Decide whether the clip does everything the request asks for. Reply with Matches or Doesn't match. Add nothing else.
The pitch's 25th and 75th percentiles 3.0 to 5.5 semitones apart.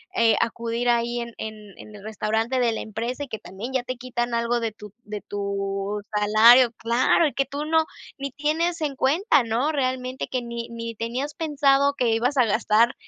Matches